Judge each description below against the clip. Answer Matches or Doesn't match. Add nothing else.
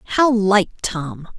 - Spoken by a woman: Matches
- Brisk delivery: Doesn't match